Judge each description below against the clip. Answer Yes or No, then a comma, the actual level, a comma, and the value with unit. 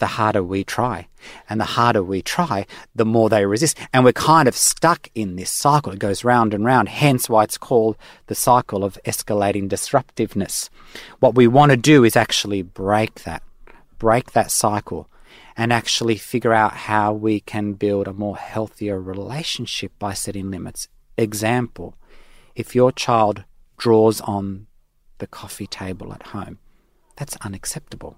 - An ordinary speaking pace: Yes, average, 160 wpm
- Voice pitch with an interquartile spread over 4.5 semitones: No, average, 3.0 semitones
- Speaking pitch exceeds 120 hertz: No, low, 105 Hz